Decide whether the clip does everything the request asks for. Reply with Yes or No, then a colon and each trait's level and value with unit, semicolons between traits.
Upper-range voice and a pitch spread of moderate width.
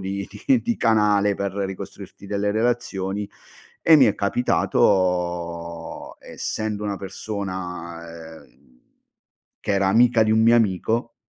No: low, 100 Hz; average, 3.0 semitones